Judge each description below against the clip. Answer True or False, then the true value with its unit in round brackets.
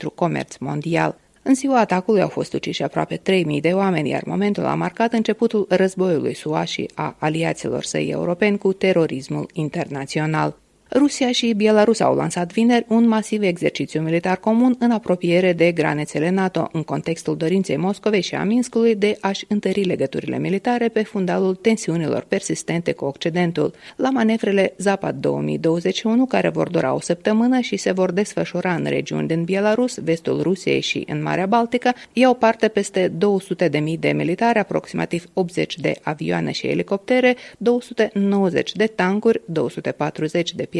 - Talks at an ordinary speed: True (150 wpm)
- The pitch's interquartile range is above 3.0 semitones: True (5.0 semitones)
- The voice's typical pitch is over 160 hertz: True (190 Hz)